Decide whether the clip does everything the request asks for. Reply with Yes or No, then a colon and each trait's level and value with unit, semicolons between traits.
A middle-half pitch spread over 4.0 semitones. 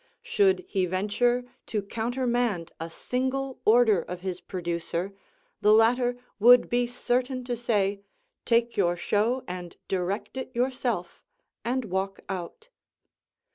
Yes: average, 4.7 semitones